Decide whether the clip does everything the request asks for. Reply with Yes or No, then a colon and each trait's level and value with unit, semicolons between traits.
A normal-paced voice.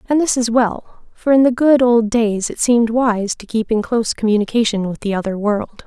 No: fast, 225 wpm